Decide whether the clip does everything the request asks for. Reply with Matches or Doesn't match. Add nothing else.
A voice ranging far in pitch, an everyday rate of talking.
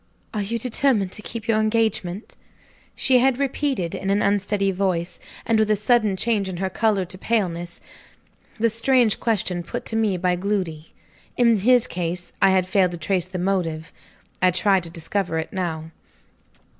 Doesn't match